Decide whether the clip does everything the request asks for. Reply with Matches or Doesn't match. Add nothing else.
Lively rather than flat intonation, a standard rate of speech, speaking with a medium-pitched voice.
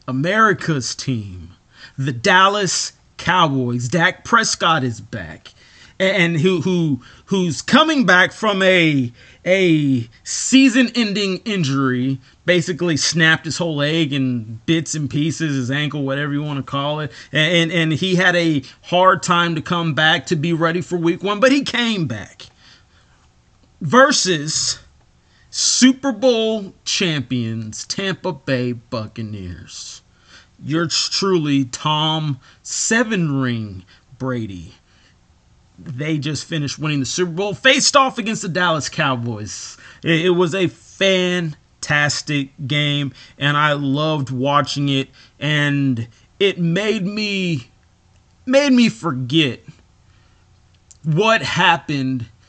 Doesn't match